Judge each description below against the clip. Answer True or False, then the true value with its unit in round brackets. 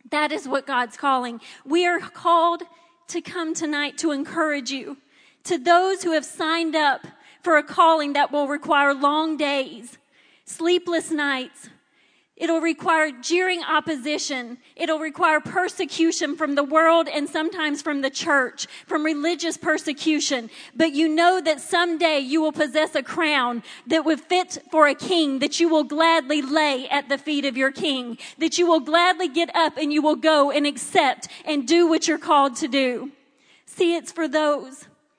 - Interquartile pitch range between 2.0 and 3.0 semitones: True (2.6 semitones)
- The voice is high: True (310 Hz)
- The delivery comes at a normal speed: True (165 wpm)